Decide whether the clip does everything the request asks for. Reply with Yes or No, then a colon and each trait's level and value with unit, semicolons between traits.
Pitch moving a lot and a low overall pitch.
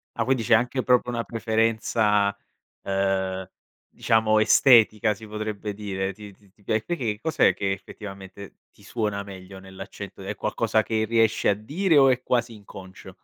No: narrow, 2.6 semitones; low, 105 Hz